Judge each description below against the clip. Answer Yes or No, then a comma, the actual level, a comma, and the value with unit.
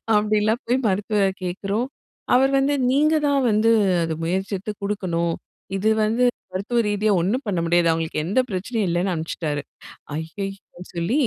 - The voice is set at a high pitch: Yes, high, 200 Hz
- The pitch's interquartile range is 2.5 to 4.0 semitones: No, average, 4.5 semitones